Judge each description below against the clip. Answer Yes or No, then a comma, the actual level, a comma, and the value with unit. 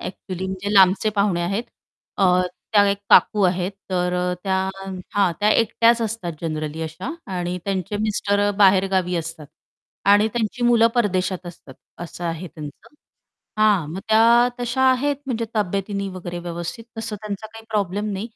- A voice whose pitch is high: Yes, high, 195 Hz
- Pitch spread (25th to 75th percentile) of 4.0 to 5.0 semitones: No, average, 3.2 semitones